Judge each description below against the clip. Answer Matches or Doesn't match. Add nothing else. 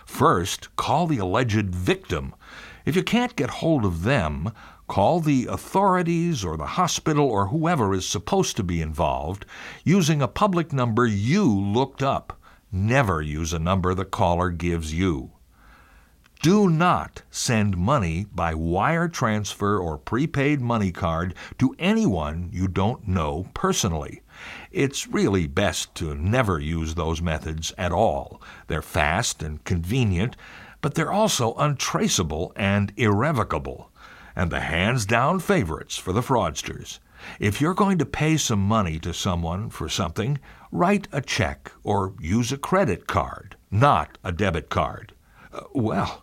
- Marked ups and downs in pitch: Matches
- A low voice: Matches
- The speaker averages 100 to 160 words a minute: Matches